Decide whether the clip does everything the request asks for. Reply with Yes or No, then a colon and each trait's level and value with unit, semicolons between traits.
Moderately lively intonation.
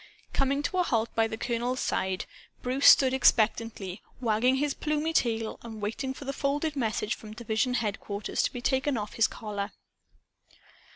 Yes: average, 3.7 semitones